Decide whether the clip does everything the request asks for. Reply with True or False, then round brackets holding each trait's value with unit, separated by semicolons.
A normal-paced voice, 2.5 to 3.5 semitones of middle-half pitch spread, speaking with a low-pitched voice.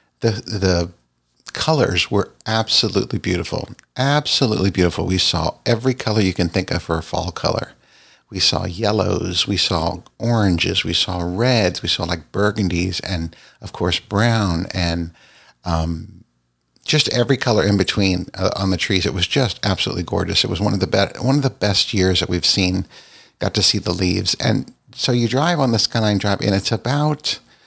False (180 wpm; 4.0 semitones; 95 Hz)